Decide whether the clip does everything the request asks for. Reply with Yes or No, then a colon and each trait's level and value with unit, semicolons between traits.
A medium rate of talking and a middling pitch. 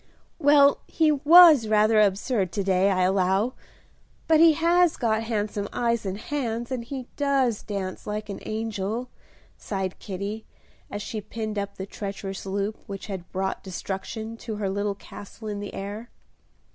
No: average, 160 wpm; high, 215 Hz